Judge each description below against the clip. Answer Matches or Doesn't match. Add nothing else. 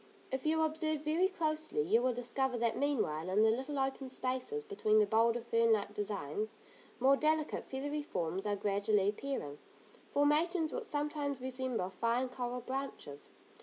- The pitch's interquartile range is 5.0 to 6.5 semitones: Matches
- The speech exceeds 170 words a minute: Doesn't match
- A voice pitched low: Doesn't match